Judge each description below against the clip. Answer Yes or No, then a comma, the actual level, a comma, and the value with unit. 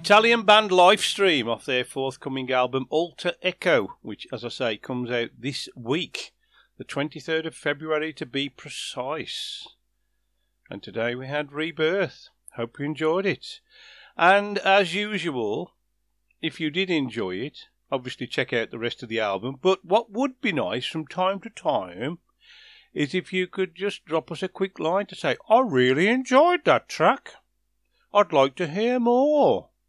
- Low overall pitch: No, medium, 170 Hz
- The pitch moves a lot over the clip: Yes, wide, 6.4 semitones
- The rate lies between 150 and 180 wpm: Yes, average, 160 wpm